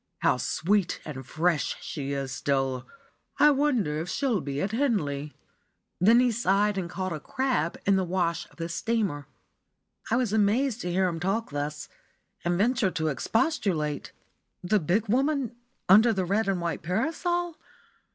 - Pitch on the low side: No, high, 190 Hz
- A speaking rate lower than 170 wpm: Yes, average, 160 wpm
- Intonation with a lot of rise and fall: Yes, wide, 6.5 semitones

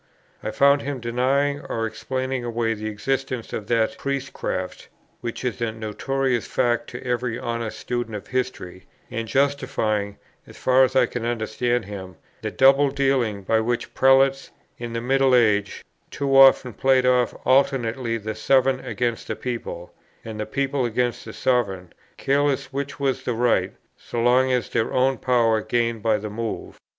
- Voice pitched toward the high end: No, low, 120 Hz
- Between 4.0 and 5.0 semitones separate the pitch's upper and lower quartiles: No, average, 2.9 semitones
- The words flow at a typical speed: Yes, average, 165 wpm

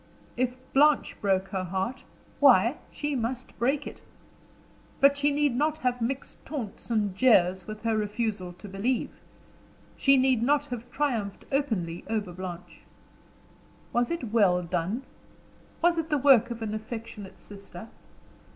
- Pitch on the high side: Yes, high, 230 Hz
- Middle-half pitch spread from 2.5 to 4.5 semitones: No, wide, 5.5 semitones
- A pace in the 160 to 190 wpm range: No, average, 140 wpm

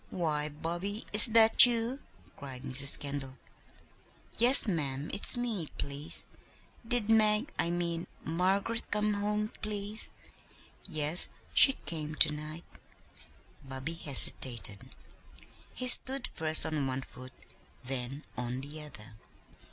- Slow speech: Yes, slow, 115 wpm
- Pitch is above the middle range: No, medium, 160 Hz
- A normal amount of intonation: No, wide, 7.1 semitones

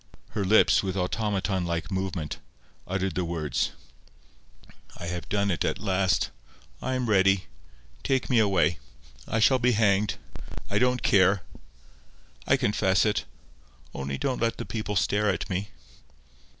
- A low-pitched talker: Yes, very low, 95 Hz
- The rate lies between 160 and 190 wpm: No, average, 140 wpm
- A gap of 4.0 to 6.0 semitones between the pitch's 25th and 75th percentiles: No, average, 2.8 semitones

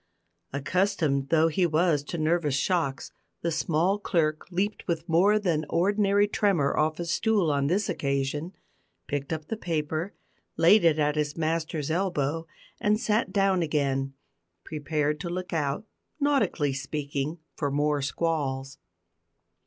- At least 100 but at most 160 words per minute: Yes, slow, 135 wpm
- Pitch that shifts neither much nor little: Yes, average, 3.9 semitones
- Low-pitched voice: No, medium, 160 Hz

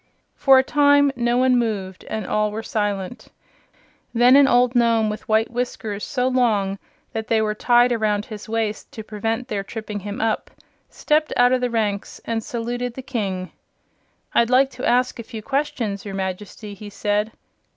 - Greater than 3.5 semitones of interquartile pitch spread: No, average, 3.0 semitones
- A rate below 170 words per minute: No, average, 175 wpm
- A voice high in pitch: Yes, high, 225 Hz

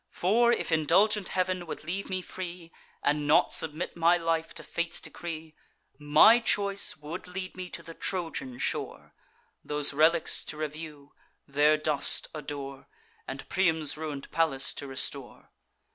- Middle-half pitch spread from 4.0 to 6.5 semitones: No, average, 3.4 semitones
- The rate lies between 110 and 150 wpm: Yes, average, 145 wpm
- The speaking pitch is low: No, medium, 160 Hz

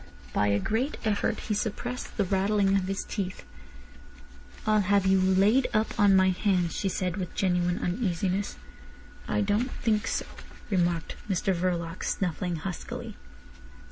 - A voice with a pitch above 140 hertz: Yes, high, 190 Hz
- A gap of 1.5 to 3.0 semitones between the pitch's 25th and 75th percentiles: Yes, narrow, 2.4 semitones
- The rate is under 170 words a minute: Yes, average, 140 wpm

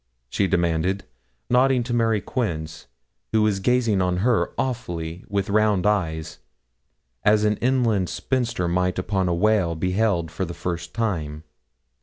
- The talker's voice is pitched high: No, very low, 95 Hz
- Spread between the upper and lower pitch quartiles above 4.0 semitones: Yes, average, 4.4 semitones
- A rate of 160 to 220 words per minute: No, average, 140 wpm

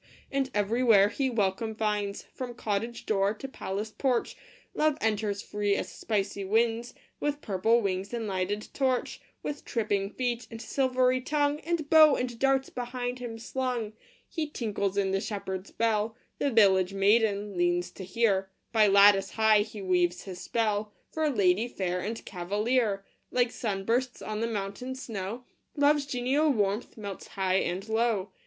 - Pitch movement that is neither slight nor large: Yes, average, 3.9 semitones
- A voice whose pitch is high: Yes, high, 220 Hz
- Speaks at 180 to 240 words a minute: No, average, 160 wpm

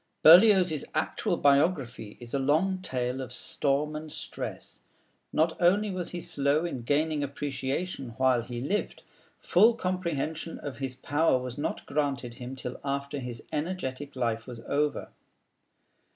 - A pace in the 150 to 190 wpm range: No, average, 140 wpm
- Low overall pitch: No, medium, 145 Hz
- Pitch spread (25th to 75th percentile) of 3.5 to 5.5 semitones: Yes, average, 4.1 semitones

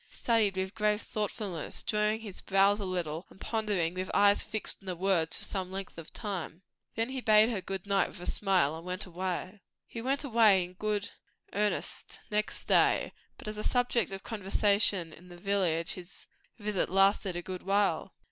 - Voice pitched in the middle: No, high, 195 Hz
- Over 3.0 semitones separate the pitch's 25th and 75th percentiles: No, narrow, 2.6 semitones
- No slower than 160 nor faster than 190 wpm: Yes, average, 185 wpm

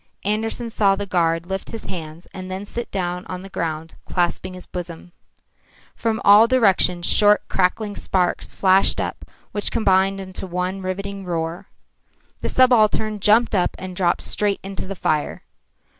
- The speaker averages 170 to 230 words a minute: No, average, 155 wpm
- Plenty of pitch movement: No, narrow, 2.5 semitones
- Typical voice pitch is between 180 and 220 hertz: Yes, high, 190 Hz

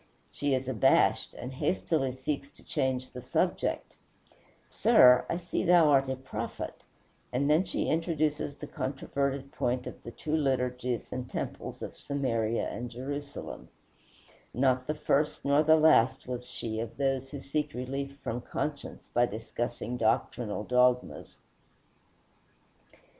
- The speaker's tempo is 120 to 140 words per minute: Yes, slow, 135 wpm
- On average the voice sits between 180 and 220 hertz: No, low, 130 Hz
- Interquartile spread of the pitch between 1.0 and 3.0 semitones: Yes, narrow, 2.5 semitones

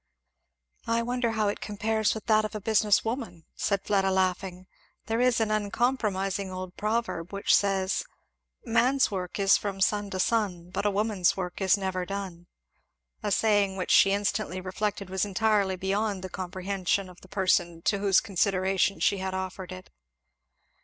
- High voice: Yes, high, 195 Hz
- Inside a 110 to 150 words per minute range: No, average, 165 wpm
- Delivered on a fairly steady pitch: Yes, narrow, 2.2 semitones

